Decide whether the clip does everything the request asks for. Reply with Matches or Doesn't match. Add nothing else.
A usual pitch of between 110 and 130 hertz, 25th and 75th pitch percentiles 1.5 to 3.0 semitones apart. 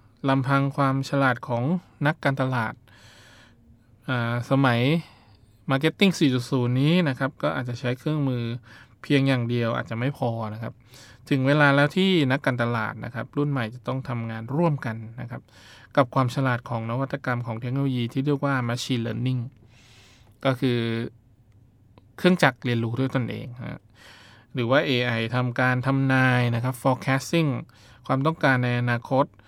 Matches